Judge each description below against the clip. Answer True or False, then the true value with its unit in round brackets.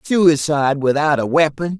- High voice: False (150 Hz)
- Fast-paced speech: False (135 wpm)